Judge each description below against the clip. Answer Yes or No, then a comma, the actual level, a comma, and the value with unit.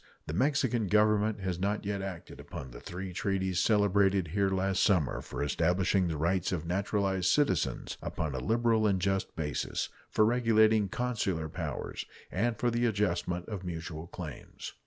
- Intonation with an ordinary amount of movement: Yes, average, 3.5 semitones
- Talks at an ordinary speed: Yes, average, 155 wpm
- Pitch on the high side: No, very low, 95 Hz